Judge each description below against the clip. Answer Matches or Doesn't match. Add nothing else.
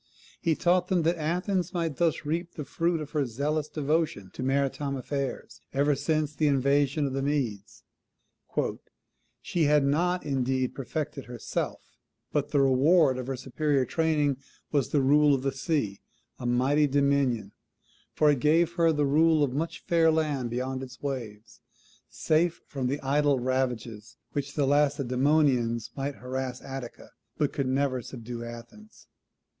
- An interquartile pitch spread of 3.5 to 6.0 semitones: Doesn't match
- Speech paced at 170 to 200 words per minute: Doesn't match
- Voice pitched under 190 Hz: Matches